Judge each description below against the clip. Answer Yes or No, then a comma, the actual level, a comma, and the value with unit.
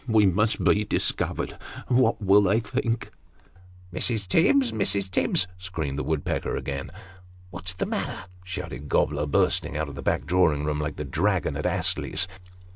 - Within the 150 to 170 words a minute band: No, average, 180 wpm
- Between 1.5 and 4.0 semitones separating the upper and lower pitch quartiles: No, average, 4.8 semitones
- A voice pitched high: No, very low, 90 Hz